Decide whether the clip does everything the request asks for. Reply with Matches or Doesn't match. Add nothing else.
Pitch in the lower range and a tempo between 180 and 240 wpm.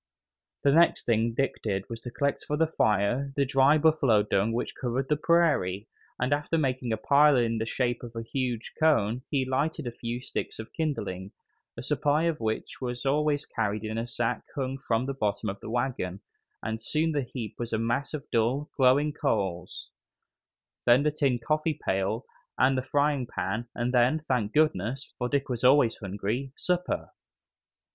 Matches